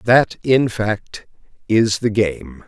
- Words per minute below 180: Yes, slow, 135 wpm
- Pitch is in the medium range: No, low, 105 Hz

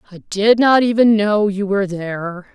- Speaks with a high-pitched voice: Yes, high, 205 Hz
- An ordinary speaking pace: Yes, average, 190 wpm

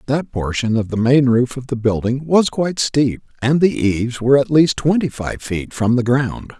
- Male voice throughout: Yes, male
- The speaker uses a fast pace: Yes, fast, 220 wpm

